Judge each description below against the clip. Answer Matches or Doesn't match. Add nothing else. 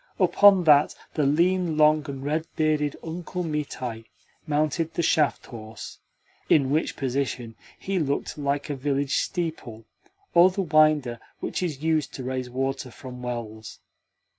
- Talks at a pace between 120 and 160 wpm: Matches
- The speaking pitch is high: Doesn't match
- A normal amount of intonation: Matches